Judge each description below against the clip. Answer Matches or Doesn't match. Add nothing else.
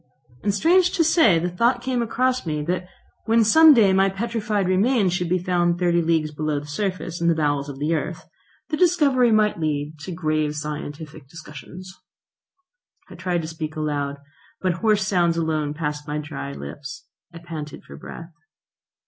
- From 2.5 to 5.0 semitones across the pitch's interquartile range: Doesn't match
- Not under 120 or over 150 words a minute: Doesn't match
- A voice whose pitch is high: Doesn't match